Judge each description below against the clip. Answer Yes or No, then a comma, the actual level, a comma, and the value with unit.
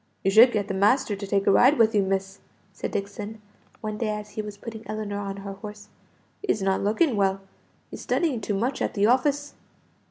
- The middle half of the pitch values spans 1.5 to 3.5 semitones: Yes, narrow, 2.4 semitones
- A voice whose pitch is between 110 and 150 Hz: No, high, 210 Hz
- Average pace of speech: No, fast, 210 wpm